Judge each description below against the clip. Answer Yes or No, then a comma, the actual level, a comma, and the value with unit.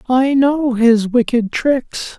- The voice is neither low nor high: No, very high, 250 Hz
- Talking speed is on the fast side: No, slow, 135 wpm